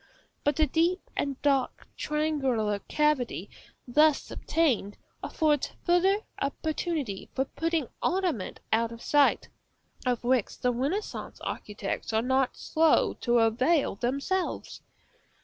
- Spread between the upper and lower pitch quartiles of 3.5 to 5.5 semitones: Yes, average, 4.8 semitones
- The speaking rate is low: Yes, slow, 115 wpm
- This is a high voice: Yes, very high, 275 Hz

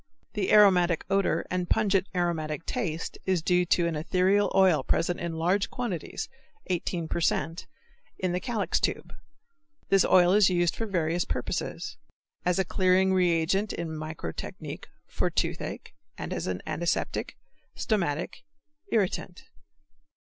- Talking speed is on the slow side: Yes, slow, 130 wpm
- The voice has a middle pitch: Yes, medium, 180 Hz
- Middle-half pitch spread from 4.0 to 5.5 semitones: No, narrow, 2.4 semitones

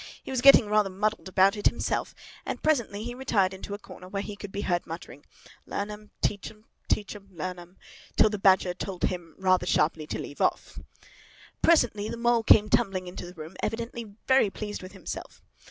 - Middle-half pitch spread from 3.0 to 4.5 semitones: No, narrow, 2.6 semitones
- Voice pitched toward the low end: No, high, 200 Hz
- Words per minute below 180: No, average, 200 wpm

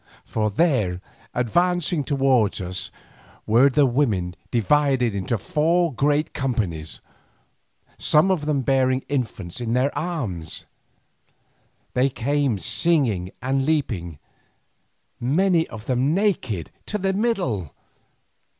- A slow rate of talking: Yes, slow, 105 wpm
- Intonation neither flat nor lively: No, wide, 5.9 semitones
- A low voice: Yes, low, 130 Hz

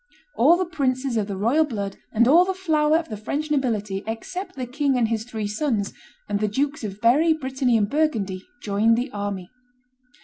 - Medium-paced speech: Yes, average, 195 wpm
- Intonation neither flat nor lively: No, wide, 6.1 semitones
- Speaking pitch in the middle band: No, high, 245 Hz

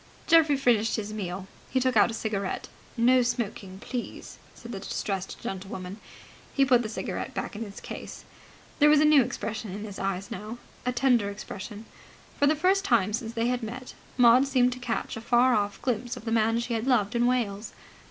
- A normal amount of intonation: Yes, average, 3.4 semitones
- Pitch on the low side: No, high, 230 Hz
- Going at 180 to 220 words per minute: Yes, average, 200 wpm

